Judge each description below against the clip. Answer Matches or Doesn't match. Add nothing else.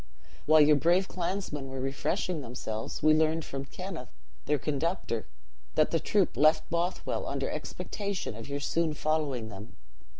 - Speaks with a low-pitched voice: Doesn't match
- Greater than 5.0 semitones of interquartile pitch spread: Doesn't match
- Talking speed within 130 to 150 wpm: Matches